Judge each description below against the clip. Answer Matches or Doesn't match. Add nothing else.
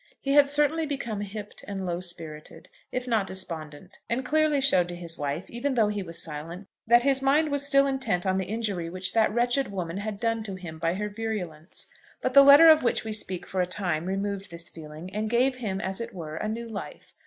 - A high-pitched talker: Matches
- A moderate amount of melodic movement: Doesn't match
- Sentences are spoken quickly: Matches